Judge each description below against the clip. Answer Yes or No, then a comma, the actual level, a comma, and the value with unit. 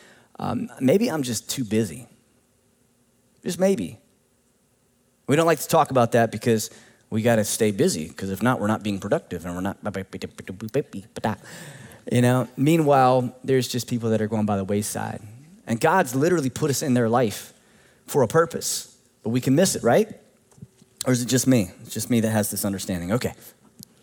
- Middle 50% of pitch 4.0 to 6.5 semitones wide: No, average, 3.4 semitones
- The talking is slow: No, average, 180 wpm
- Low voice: Yes, low, 120 Hz